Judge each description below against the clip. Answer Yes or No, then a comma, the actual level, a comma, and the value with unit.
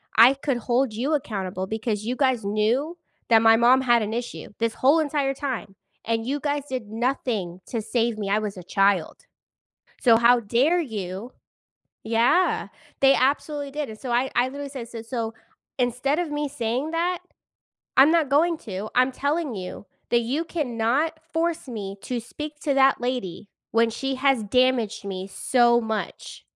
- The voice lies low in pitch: No, high, 245 Hz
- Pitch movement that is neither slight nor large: Yes, average, 3.9 semitones